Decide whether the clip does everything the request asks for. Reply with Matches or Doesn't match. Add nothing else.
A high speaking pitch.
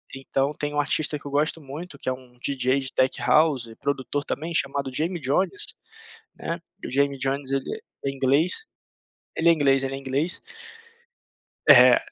Doesn't match